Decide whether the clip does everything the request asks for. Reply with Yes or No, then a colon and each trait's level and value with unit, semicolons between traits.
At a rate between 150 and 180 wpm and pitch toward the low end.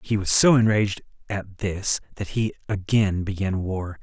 Yes: average, 165 wpm; low, 100 Hz